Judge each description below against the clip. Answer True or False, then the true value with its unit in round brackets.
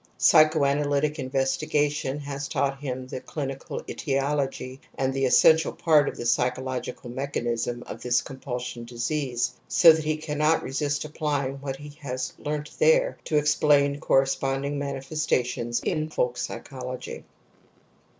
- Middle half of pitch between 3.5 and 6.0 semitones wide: False (2.4 semitones)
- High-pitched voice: False (140 Hz)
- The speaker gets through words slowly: True (125 wpm)